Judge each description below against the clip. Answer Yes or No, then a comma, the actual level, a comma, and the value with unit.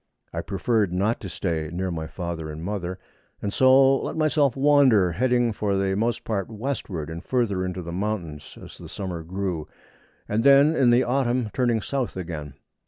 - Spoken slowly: No, average, 175 wpm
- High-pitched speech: No, low, 100 Hz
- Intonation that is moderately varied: No, wide, 6.0 semitones